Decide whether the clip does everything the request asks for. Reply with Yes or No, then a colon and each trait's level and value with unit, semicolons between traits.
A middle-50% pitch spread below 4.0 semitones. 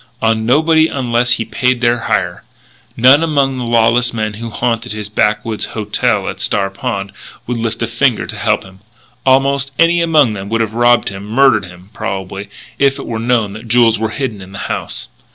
Yes: average, 3.2 semitones